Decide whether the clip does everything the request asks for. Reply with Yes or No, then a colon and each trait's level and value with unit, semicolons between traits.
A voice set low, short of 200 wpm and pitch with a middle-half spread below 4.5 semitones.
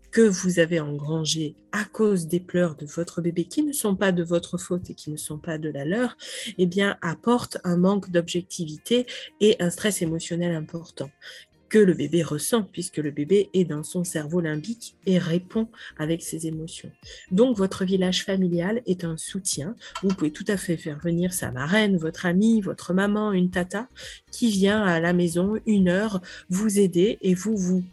No: medium, 180 Hz; average, 185 wpm; average, 3.2 semitones